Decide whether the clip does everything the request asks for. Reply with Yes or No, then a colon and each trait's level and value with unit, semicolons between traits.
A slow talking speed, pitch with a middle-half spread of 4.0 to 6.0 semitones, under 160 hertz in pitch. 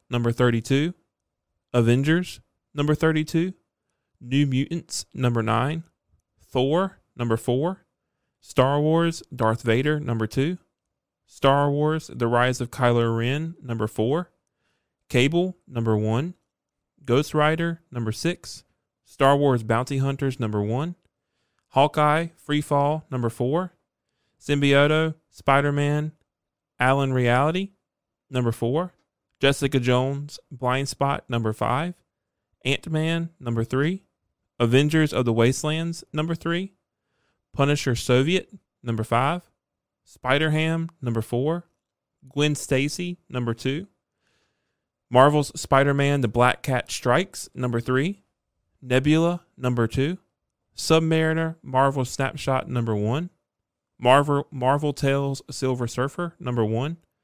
Yes: slow, 105 wpm; average, 4.7 semitones; low, 135 Hz